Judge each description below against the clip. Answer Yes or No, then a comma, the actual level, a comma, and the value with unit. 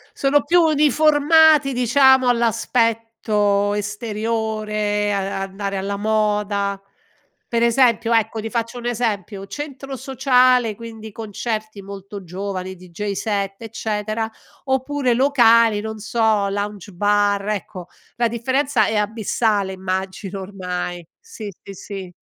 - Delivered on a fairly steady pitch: No, average, 3.1 semitones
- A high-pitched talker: Yes, high, 215 Hz